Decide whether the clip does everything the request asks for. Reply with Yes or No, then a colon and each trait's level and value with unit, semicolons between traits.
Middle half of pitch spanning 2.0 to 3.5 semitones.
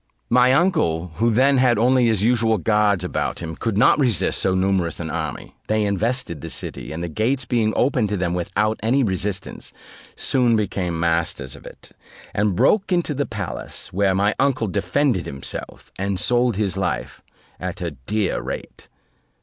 No: average, 5.2 semitones